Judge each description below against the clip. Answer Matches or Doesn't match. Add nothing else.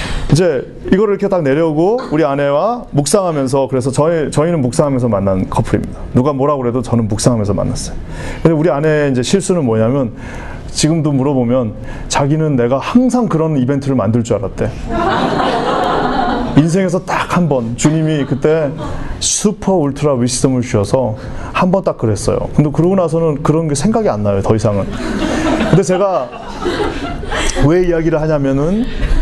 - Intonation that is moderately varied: Matches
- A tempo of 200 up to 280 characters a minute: Doesn't match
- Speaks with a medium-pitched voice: Matches